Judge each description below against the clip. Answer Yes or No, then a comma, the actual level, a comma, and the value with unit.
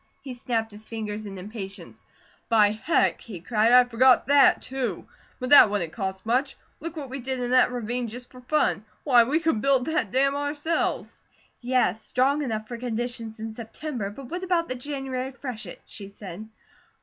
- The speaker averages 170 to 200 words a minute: Yes, average, 180 wpm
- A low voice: No, high, 245 Hz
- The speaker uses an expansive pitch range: No, average, 3.7 semitones